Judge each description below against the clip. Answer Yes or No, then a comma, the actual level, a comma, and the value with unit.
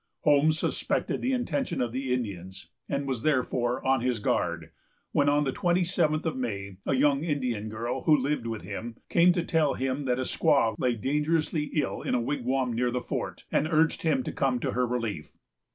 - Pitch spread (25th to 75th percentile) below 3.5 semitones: No, average, 3.9 semitones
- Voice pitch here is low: Yes, low, 130 Hz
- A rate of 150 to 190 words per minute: No, average, 200 wpm